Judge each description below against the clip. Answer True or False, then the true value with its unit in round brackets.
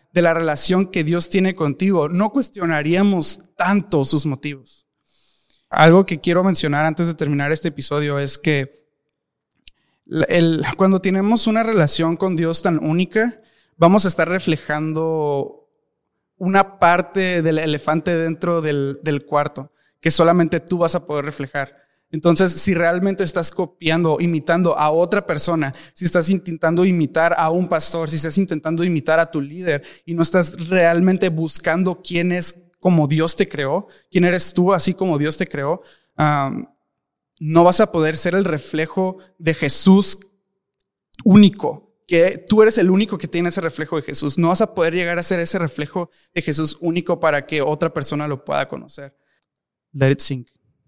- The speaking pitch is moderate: True (170 Hz)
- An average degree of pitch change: True (3.2 semitones)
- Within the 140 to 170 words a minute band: True (160 wpm)